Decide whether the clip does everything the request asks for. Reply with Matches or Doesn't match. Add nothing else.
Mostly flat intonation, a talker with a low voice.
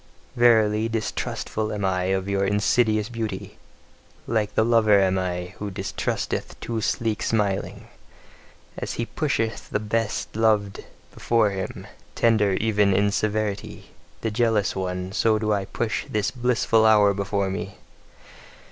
Matches